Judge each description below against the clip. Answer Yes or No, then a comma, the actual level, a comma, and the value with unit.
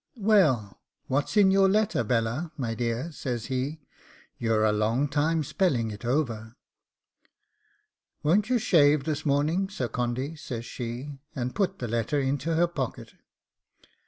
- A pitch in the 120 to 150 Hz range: Yes, medium, 140 Hz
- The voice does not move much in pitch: No, wide, 5.5 semitones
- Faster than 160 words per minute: No, average, 140 wpm